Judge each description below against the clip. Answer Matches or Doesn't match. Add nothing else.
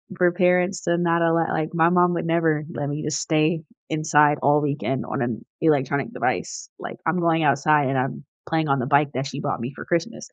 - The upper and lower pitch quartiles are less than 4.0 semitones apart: Matches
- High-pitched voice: Doesn't match